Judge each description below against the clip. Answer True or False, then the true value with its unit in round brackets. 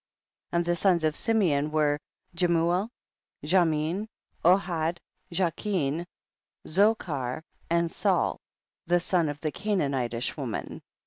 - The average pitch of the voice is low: False (170 Hz)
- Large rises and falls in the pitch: False (3.3 semitones)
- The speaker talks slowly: True (110 wpm)